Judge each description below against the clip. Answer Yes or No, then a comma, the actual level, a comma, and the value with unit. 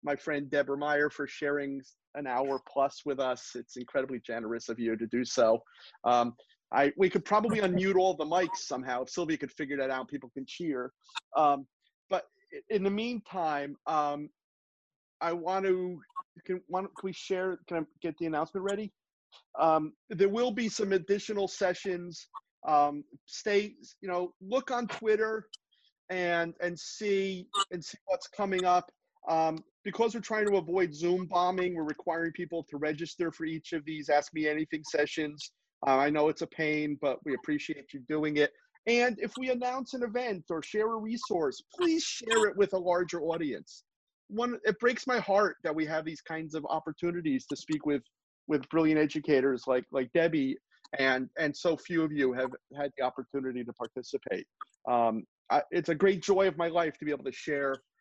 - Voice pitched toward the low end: No, medium, 170 Hz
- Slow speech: No, average, 180 wpm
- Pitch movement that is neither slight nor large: No, wide, 5.7 semitones